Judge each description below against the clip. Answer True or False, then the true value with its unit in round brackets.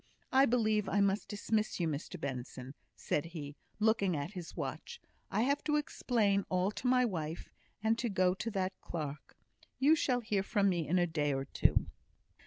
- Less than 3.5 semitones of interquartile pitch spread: False (5.6 semitones)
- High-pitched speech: True (195 Hz)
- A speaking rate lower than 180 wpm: False (185 wpm)